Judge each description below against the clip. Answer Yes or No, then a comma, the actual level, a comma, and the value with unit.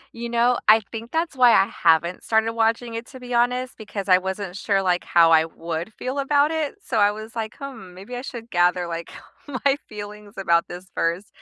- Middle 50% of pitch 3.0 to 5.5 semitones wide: Yes, average, 5.0 semitones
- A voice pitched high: Yes, high, 215 Hz